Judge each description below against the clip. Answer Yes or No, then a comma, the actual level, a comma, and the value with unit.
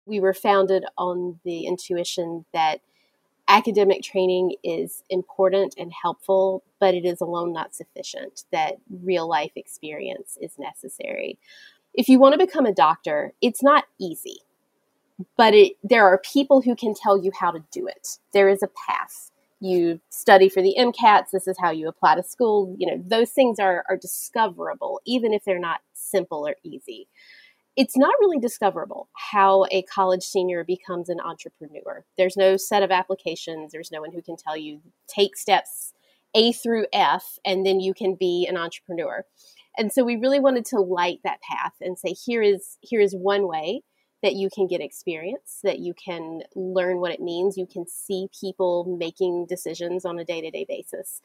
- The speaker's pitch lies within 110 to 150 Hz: No, high, 190 Hz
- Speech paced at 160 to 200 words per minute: Yes, average, 175 wpm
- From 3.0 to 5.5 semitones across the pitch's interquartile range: Yes, average, 3.4 semitones